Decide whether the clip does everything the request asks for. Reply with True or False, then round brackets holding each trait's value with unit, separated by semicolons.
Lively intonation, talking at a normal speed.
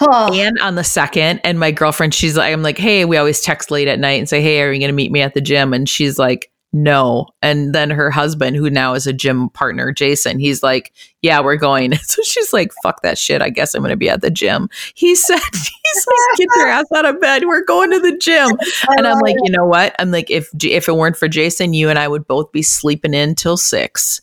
False (5.7 semitones; 260 wpm)